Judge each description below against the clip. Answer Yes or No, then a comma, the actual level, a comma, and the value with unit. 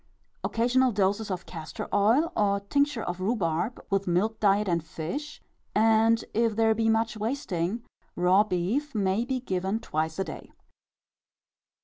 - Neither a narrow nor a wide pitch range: Yes, average, 3.6 semitones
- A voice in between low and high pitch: No, high, 210 Hz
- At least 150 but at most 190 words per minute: No, average, 140 wpm